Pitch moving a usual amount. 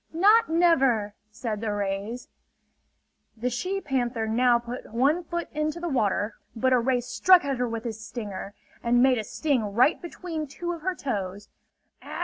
No: wide, 5.8 semitones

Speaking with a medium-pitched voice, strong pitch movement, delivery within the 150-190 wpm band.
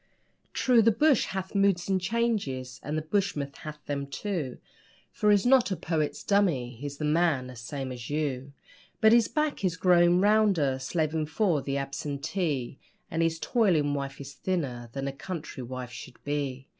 Yes: medium, 155 Hz; wide, 5.9 semitones; average, 170 wpm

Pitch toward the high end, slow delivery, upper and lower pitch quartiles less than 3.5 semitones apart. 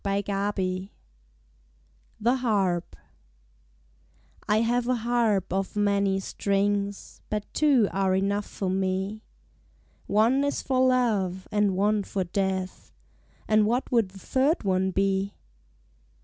Yes: high, 200 Hz; slow, 115 wpm; average, 2.8 semitones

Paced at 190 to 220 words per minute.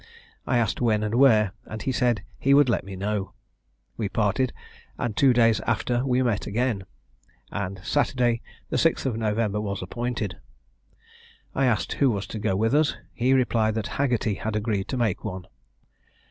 No: average, 175 wpm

